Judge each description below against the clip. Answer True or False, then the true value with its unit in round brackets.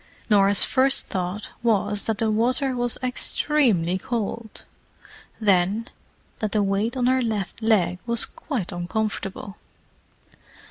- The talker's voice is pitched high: True (215 Hz)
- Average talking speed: False (120 wpm)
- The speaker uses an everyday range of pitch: True (3.5 semitones)